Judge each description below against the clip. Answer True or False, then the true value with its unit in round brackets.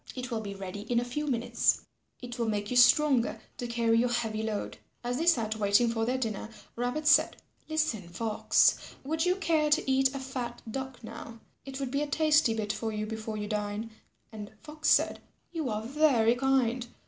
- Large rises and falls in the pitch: False (3.5 semitones)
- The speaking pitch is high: True (240 Hz)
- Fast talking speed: False (195 wpm)